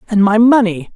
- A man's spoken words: Yes, male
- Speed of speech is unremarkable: Yes, average, 190 wpm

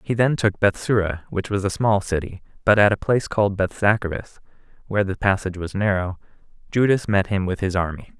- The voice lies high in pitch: No, low, 100 Hz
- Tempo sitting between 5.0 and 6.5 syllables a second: Yes, 5.9 syllables/s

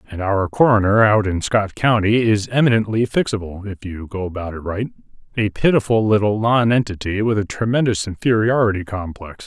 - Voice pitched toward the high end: No, low, 105 Hz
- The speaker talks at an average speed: Yes, average, 160 wpm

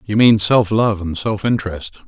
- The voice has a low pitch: Yes, low, 100 Hz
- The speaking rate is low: No, average, 200 wpm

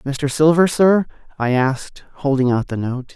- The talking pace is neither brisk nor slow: Yes, average, 170 wpm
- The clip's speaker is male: Yes, male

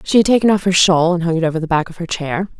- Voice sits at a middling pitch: Yes, medium, 175 Hz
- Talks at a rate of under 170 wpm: No, fast, 345 wpm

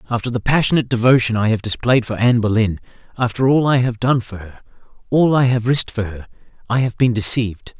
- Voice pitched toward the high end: No, low, 115 Hz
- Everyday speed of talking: Yes, average, 185 wpm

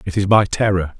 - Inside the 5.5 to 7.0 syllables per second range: Yes, 5.8 syllables/s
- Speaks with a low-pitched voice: Yes, very low, 95 Hz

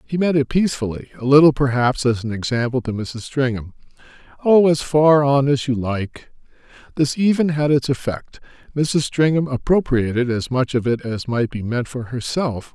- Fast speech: No, average, 175 wpm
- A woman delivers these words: No, male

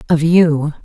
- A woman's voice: Yes, female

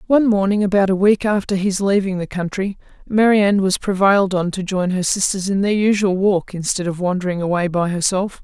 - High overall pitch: Yes, high, 195 Hz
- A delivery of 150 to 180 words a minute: No, average, 200 wpm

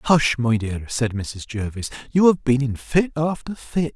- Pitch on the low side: Yes, low, 130 Hz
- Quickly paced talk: No, average, 195 wpm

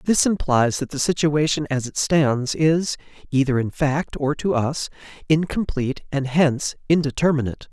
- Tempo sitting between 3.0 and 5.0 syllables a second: Yes, 4.8 syllables/s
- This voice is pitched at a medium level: Yes, medium, 145 Hz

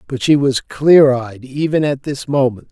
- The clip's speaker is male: Yes, male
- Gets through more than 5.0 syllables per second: No, 4.3 syllables/s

